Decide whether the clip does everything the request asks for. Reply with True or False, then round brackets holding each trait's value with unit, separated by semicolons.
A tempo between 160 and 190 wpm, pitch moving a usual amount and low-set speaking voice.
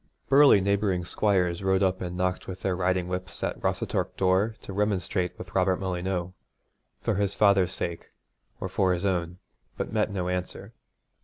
False (165 wpm; 1.7 semitones; 95 Hz)